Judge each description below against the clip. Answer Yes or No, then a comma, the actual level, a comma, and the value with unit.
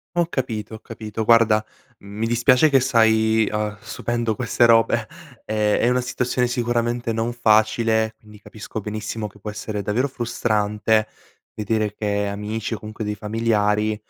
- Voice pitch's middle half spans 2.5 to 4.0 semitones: No, narrow, 1.9 semitones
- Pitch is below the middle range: Yes, low, 110 Hz